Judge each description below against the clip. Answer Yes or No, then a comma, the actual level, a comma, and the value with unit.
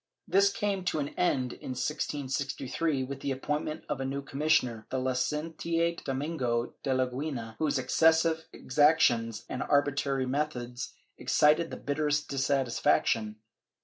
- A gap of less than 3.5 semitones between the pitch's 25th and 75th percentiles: Yes, average, 3.1 semitones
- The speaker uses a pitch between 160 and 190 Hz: No, medium, 140 Hz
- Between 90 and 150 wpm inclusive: Yes, average, 140 wpm